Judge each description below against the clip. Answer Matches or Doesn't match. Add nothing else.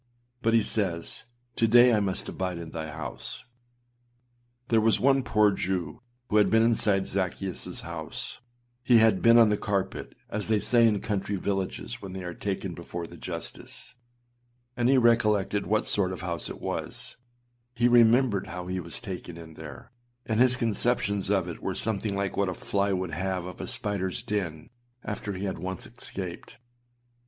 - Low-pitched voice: Matches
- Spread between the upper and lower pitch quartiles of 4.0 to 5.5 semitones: Doesn't match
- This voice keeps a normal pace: Matches